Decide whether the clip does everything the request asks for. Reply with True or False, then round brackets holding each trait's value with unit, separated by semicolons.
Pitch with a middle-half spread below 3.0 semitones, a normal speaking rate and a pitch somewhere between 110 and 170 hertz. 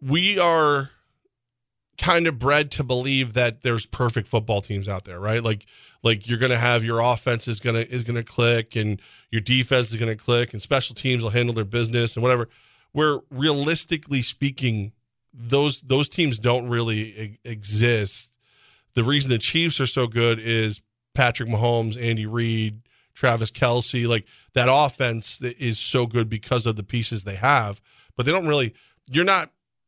True (2.4 semitones; 180 wpm; 120 Hz)